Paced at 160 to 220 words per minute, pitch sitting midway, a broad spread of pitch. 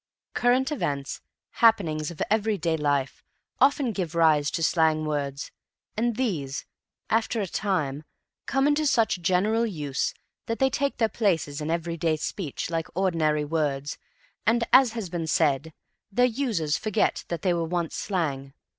No: average, 145 wpm; medium, 170 Hz; wide, 6.7 semitones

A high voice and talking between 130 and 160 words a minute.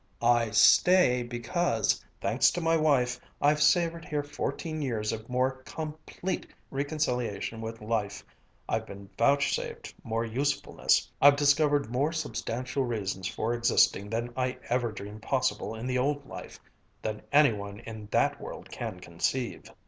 No: low, 125 Hz; average, 140 wpm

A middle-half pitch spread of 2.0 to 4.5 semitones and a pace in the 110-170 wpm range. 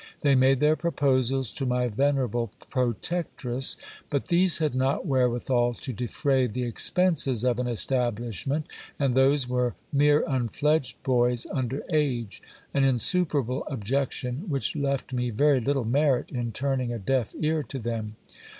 Yes: average, 2.7 semitones; average, 140 wpm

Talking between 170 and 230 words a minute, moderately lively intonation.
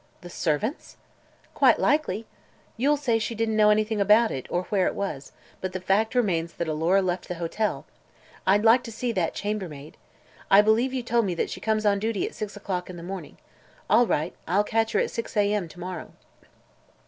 Yes: average, 200 wpm; average, 3.8 semitones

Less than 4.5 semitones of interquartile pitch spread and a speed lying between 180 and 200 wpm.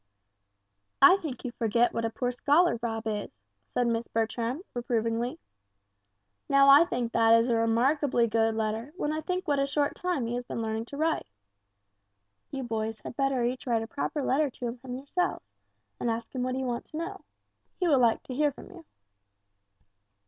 Yes: average, 3.8 semitones; average, 185 wpm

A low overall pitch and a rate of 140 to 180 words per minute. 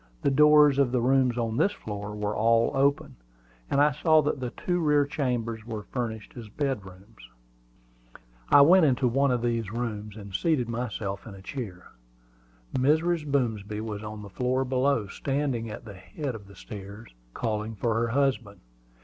Yes: low, 120 Hz; average, 170 wpm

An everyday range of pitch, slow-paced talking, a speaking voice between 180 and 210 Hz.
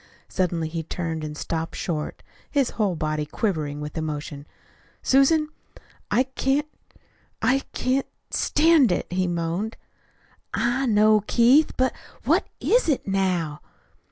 No: wide, 8.4 semitones; slow, 125 wpm; high, 190 Hz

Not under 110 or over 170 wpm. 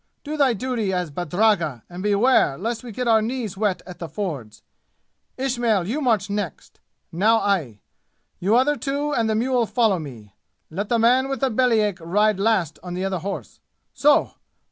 No: average, 180 wpm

